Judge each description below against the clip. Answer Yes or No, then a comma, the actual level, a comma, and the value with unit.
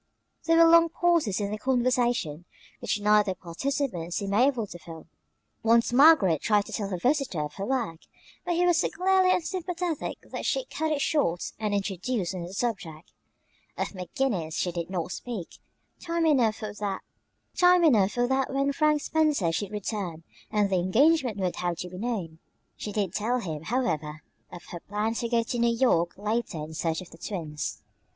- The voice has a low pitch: No, high, 215 Hz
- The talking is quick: No, average, 175 wpm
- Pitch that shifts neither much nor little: No, wide, 7.3 semitones